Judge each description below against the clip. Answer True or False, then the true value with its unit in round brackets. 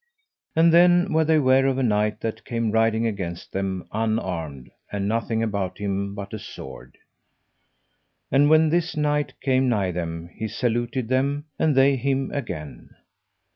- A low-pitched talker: True (115 Hz)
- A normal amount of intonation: False (5.8 semitones)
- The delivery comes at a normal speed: True (155 wpm)